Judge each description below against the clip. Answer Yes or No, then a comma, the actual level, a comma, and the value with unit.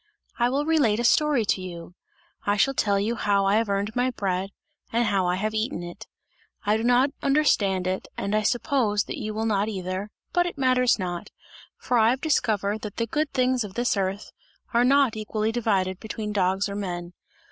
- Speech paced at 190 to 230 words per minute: Yes, average, 200 wpm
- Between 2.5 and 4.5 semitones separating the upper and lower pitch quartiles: Yes, average, 3.8 semitones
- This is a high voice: Yes, high, 215 Hz